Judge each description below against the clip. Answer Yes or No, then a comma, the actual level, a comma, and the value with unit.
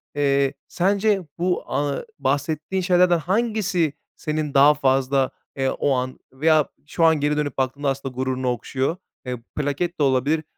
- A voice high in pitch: No, medium, 145 Hz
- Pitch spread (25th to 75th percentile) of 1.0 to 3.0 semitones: No, average, 3.9 semitones